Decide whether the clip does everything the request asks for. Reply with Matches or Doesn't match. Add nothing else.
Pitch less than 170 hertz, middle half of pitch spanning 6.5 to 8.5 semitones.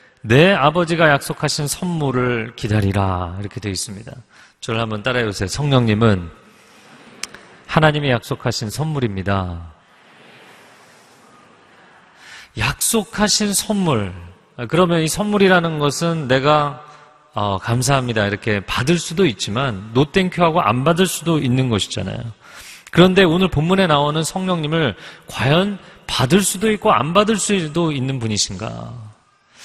Matches